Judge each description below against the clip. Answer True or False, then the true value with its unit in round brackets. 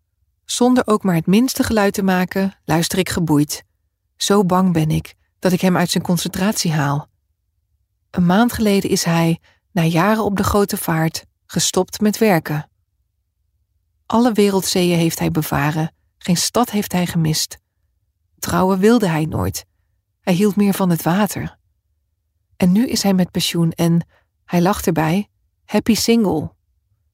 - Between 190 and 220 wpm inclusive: False (150 wpm)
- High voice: False (170 Hz)